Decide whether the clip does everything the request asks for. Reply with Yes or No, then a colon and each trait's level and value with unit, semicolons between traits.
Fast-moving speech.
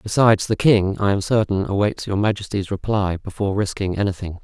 No: average, 175 wpm